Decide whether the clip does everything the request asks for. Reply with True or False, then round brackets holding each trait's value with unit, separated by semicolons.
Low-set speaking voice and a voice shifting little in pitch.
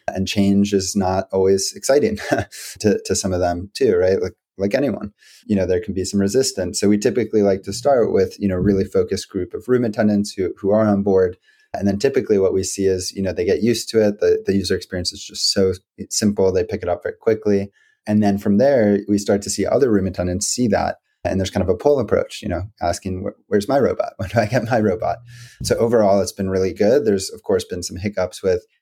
True (100 Hz; 1.8 semitones)